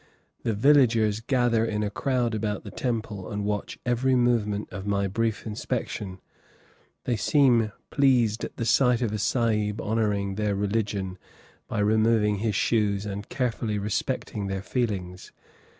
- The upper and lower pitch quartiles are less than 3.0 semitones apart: Yes, narrow, 2.4 semitones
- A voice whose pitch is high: No, low, 110 Hz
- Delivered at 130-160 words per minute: Yes, average, 145 wpm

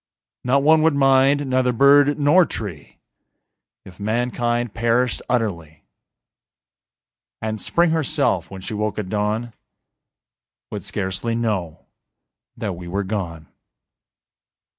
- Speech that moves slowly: Yes, slow, 110 wpm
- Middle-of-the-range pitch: No, low, 115 Hz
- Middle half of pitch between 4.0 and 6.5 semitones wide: Yes, average, 5.3 semitones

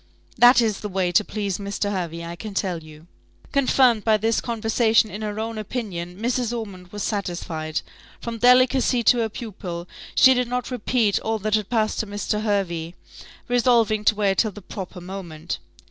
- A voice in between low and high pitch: No, high, 215 Hz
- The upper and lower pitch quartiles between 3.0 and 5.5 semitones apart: Yes, average, 3.6 semitones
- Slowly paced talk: No, average, 175 wpm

